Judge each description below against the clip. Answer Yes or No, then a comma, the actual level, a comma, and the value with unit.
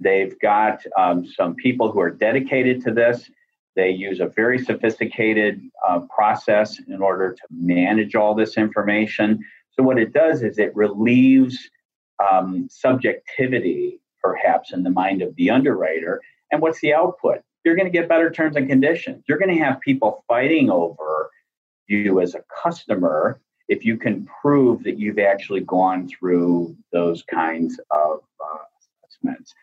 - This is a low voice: Yes, low, 115 Hz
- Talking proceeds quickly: No, average, 155 wpm